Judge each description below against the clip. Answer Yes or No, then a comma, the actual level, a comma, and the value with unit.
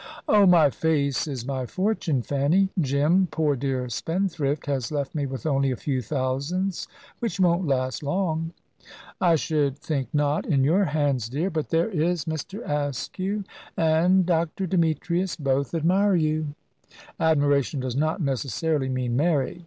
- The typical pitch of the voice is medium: Yes, medium, 155 Hz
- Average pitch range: Yes, average, 3.9 semitones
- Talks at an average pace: Yes, average, 145 wpm